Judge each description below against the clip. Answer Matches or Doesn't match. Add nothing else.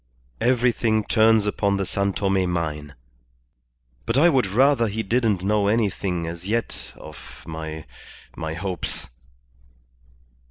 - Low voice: Matches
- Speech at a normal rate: Doesn't match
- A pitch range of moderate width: Matches